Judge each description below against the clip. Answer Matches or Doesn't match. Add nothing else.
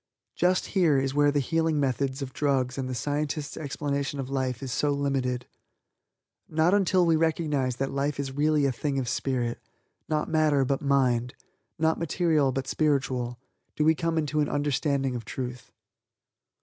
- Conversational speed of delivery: Matches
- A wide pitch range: Doesn't match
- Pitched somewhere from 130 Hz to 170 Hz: Matches